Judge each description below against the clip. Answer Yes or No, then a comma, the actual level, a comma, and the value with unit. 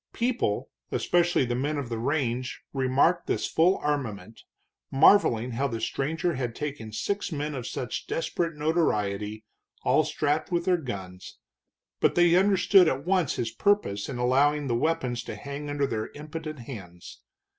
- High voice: No, medium, 140 Hz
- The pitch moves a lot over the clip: Yes, wide, 5.8 semitones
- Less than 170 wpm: Yes, average, 155 wpm